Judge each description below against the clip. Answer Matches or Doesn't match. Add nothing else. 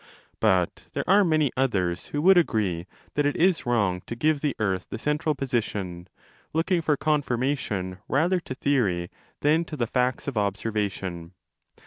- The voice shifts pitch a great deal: Matches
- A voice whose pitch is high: Doesn't match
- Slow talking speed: Doesn't match